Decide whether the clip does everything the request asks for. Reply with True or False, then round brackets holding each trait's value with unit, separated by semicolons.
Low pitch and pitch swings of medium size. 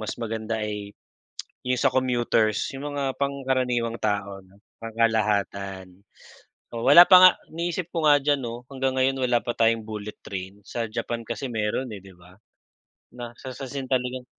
True (120 Hz; 3.8 semitones)